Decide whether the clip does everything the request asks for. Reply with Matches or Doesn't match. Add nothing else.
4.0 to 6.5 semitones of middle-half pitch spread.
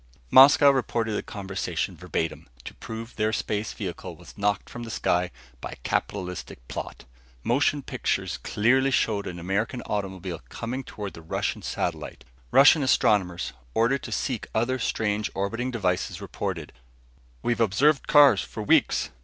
Matches